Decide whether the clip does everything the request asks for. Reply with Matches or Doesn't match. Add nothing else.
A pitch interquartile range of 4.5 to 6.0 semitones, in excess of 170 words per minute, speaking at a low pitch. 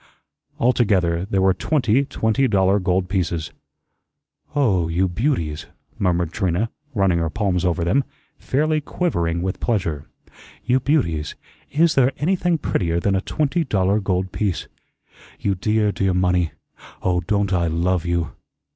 Doesn't match